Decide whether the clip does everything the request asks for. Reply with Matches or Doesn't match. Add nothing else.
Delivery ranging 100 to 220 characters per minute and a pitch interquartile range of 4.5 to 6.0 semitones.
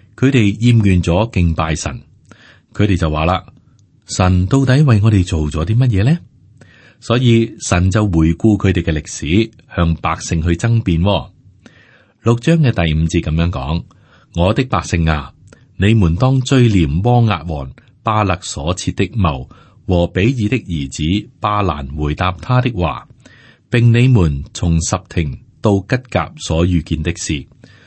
Matches